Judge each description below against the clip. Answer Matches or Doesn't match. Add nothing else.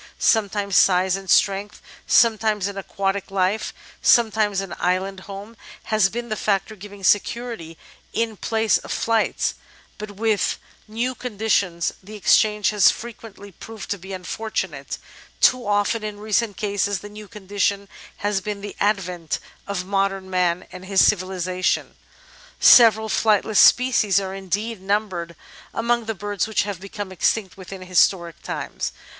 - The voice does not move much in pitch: Matches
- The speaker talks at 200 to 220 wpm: Doesn't match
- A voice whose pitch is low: Doesn't match